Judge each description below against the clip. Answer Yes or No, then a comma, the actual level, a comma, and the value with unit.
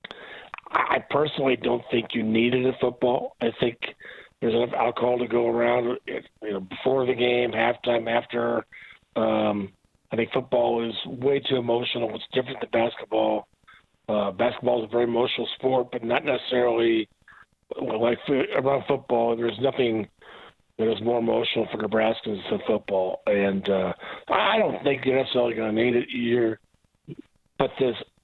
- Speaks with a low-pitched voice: Yes, low, 120 Hz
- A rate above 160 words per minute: No, average, 155 wpm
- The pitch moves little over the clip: Yes, narrow, 1.8 semitones